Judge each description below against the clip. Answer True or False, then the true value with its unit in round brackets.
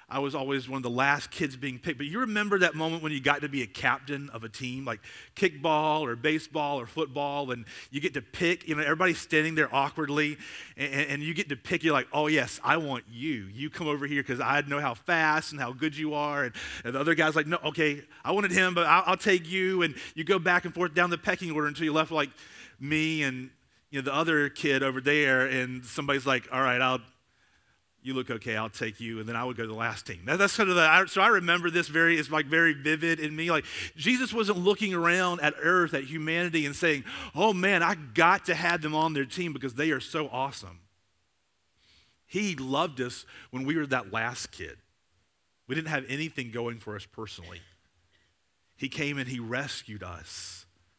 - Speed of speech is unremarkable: False (230 wpm)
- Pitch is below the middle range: False (145 Hz)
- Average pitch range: True (4.5 semitones)